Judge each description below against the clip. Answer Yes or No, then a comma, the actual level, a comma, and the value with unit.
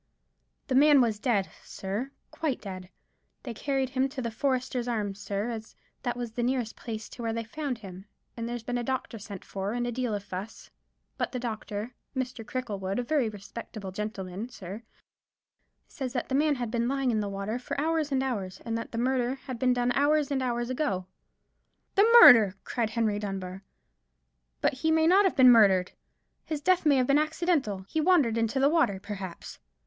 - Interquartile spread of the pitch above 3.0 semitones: Yes, average, 4.2 semitones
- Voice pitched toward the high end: Yes, high, 240 Hz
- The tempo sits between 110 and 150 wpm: No, average, 190 wpm